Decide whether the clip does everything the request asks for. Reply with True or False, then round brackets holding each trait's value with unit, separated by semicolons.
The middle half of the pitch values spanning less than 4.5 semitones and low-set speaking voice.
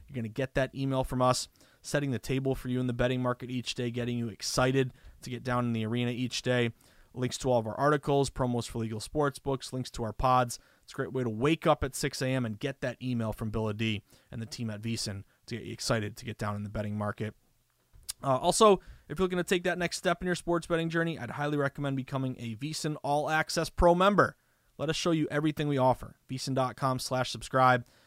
True (3.6 semitones; 130 Hz)